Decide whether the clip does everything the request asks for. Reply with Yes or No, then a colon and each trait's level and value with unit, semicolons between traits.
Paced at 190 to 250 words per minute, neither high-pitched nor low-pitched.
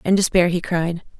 Yes: average, 200 wpm; medium, 175 Hz